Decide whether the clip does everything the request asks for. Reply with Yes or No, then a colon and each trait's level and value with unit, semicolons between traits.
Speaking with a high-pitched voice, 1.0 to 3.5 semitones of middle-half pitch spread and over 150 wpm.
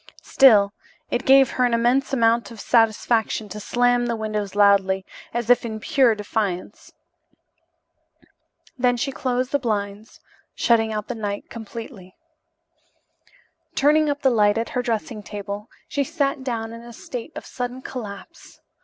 No: high, 230 Hz; average, 3.1 semitones; average, 145 wpm